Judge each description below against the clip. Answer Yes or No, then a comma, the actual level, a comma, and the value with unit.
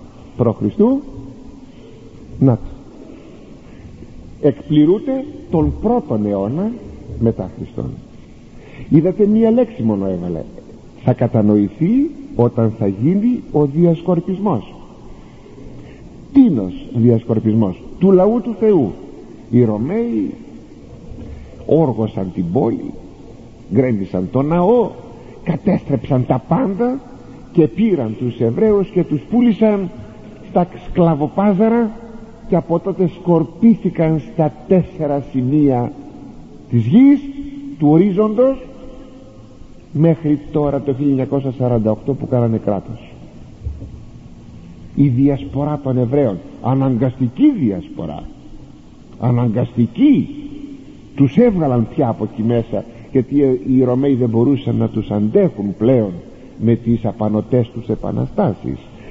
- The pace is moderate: No, slow, 95 wpm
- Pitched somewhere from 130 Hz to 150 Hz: Yes, medium, 140 Hz